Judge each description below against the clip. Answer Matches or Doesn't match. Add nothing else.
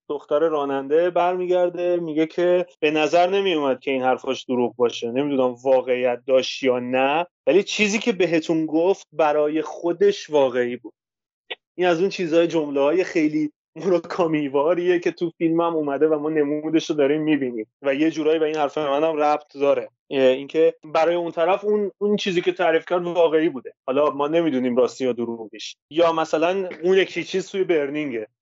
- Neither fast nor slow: Doesn't match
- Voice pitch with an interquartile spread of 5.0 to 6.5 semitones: Doesn't match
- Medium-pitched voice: Matches